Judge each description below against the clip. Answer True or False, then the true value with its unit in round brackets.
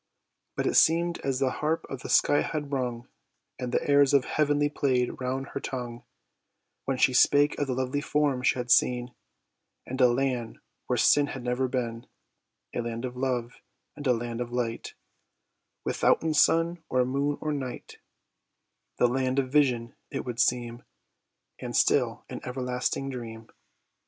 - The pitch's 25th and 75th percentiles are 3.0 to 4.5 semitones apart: False (2.5 semitones)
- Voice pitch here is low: True (130 Hz)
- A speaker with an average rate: True (160 wpm)